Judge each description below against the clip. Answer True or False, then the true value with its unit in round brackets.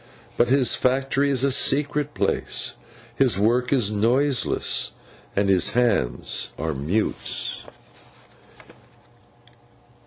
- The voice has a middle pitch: False (125 Hz)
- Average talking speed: False (95 wpm)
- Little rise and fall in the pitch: False (5.1 semitones)